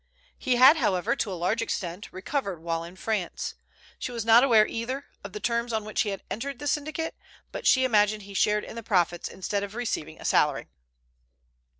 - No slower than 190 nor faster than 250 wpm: Yes, average, 200 wpm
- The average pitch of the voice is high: Yes, high, 215 Hz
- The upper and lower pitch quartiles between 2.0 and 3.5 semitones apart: No, average, 4.6 semitones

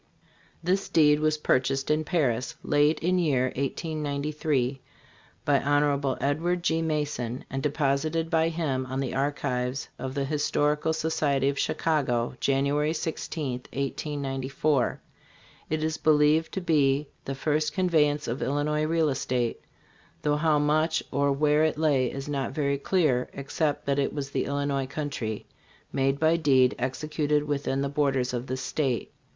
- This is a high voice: No, medium, 145 Hz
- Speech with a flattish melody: Yes, narrow, 2.3 semitones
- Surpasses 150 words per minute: No, average, 145 wpm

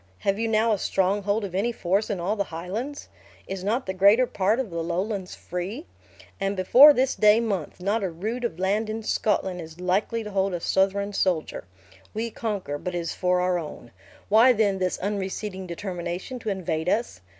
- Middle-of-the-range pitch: No, high, 195 Hz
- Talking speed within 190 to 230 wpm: Yes, average, 195 wpm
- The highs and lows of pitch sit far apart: No, average, 3.3 semitones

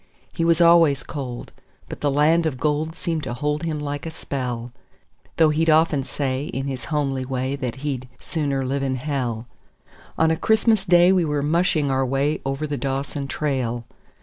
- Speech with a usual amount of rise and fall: Yes, average, 3.1 semitones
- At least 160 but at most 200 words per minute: Yes, average, 180 wpm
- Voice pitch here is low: No, medium, 145 Hz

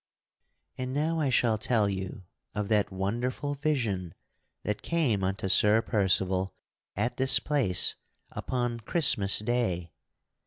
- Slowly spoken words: Yes, slow, 120 wpm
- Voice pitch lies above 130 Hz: No, low, 110 Hz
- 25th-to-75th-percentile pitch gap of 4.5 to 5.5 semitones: Yes, average, 4.8 semitones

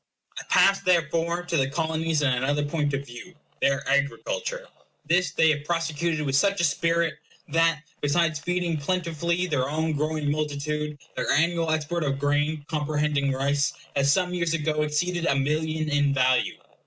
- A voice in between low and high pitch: Yes, medium, 155 Hz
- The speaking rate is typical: Yes, average, 160 wpm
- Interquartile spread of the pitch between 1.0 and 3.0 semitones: Yes, average, 2.7 semitones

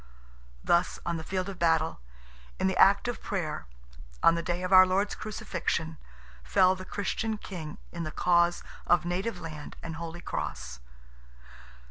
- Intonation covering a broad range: No, narrow, 2.5 semitones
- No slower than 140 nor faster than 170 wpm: Yes, average, 155 wpm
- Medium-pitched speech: Yes, medium, 175 Hz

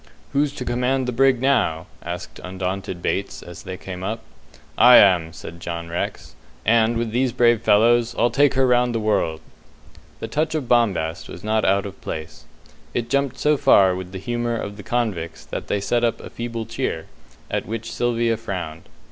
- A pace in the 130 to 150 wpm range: No, average, 185 wpm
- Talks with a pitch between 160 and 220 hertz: No, low, 115 Hz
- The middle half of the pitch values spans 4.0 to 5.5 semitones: Yes, average, 4.7 semitones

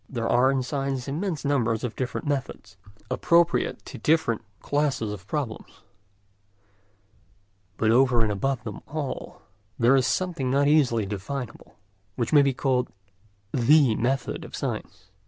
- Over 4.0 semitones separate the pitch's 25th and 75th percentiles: No, average, 3.7 semitones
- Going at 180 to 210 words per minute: No, slow, 135 wpm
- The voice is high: No, low, 130 Hz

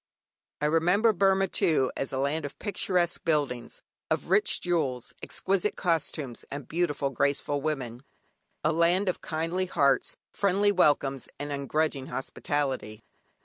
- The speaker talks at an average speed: No, slow, 130 wpm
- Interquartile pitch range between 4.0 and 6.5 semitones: Yes, average, 4.5 semitones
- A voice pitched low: No, medium, 155 Hz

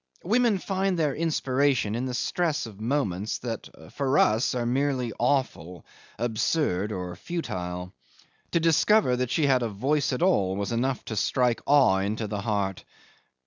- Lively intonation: Yes, wide, 5.8 semitones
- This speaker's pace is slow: No, average, 155 wpm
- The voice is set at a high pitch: No, low, 125 Hz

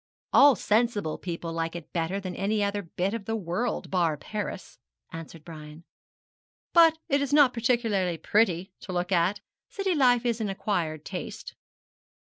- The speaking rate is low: No, average, 155 wpm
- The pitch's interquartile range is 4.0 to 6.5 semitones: Yes, wide, 5.5 semitones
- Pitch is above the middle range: Yes, high, 195 Hz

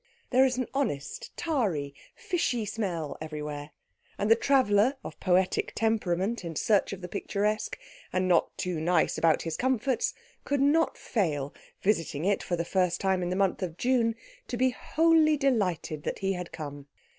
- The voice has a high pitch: Yes, high, 195 Hz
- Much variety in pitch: Yes, wide, 6.8 semitones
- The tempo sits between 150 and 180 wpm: Yes, average, 170 wpm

